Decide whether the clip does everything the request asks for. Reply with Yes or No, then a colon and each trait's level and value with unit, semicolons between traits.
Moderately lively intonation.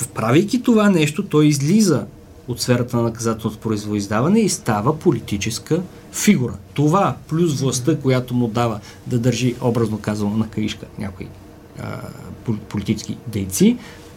No: wide, 6.5 semitones